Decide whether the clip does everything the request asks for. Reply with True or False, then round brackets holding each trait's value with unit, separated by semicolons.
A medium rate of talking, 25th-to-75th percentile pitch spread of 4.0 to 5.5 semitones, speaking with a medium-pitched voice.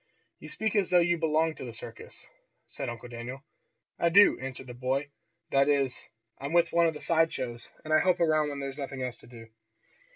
False (215 wpm; 4.4 semitones; 145 Hz)